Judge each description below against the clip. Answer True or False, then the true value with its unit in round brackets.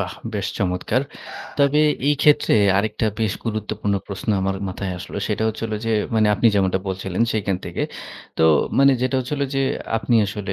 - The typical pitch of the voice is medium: False (105 Hz)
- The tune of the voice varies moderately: True (3.3 semitones)